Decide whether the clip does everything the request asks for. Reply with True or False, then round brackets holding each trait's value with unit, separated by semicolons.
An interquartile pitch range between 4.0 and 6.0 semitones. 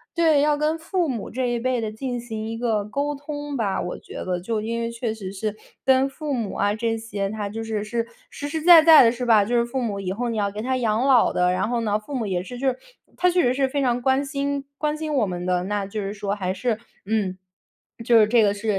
True (4.4 semitones)